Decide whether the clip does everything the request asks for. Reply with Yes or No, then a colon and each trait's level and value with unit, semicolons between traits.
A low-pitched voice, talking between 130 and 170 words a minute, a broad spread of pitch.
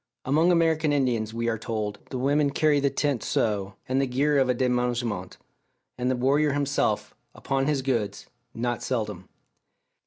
No: low, 130 Hz; average, 160 wpm; average, 3.7 semitones